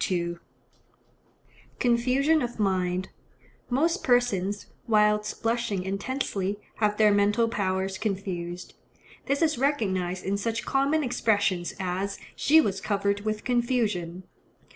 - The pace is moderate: No, slow, 100 wpm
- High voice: Yes, high, 210 Hz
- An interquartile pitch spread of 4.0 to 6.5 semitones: Yes, average, 4.3 semitones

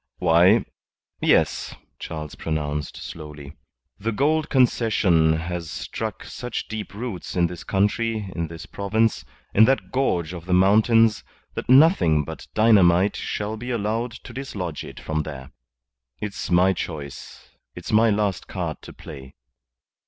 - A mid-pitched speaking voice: No, very low, 95 Hz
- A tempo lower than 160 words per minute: Yes, slow, 135 wpm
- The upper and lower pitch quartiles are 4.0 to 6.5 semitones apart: Yes, wide, 5.6 semitones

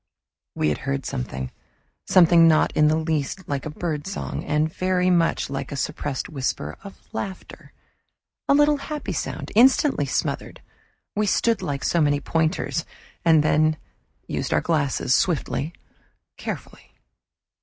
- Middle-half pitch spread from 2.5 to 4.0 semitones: No, average, 4.4 semitones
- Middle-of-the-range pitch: Yes, medium, 155 Hz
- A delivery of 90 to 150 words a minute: Yes, slow, 135 wpm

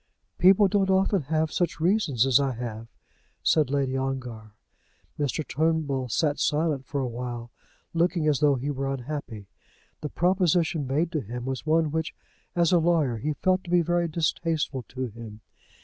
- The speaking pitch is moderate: Yes, medium, 150 Hz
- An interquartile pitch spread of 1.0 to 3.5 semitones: No, average, 4.4 semitones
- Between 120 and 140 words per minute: No, average, 165 wpm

